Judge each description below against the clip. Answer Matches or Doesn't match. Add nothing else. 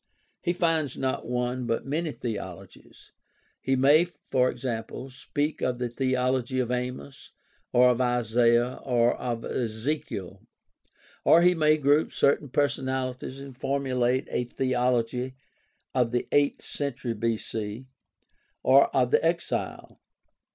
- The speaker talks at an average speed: Doesn't match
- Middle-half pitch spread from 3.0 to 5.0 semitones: Doesn't match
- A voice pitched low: Matches